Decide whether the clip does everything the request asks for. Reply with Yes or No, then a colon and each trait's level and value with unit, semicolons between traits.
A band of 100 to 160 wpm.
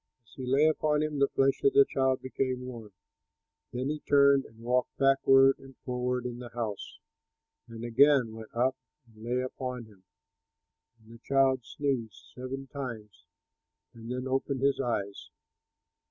Yes: average, 155 wpm